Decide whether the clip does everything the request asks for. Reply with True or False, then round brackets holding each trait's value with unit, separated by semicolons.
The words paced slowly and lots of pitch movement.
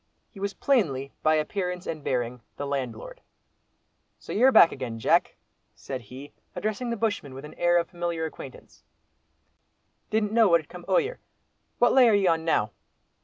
False (170 wpm; 7.4 semitones)